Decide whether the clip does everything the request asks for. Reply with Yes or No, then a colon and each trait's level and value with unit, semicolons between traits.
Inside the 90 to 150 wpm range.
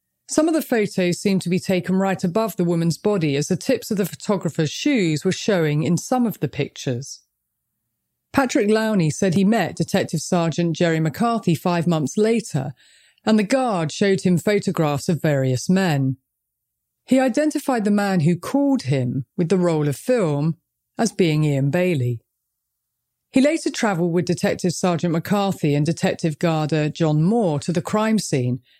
No: average, 165 wpm